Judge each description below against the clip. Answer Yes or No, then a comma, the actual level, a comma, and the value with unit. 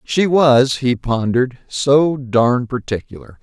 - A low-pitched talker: Yes, low, 130 Hz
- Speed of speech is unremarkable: No, slow, 125 wpm